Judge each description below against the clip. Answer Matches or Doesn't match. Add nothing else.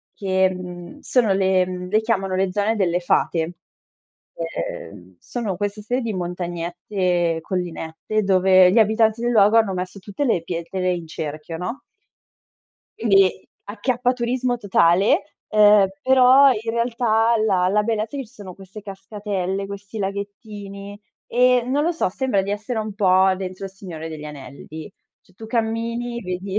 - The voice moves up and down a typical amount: Matches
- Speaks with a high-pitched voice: Matches